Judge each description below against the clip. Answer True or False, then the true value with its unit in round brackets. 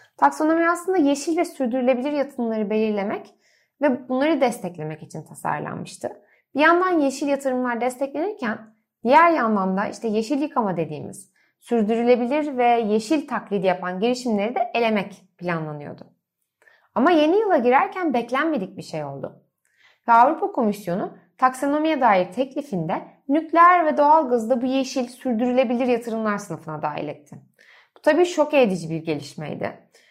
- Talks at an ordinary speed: True (125 wpm)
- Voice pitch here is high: True (250 Hz)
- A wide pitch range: True (6.1 semitones)